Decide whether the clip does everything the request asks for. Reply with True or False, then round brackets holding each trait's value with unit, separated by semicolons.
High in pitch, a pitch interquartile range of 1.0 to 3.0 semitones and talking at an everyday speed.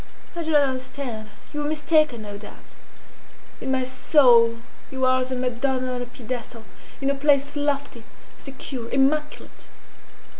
True (260 Hz; 2.6 semitones; 150 wpm)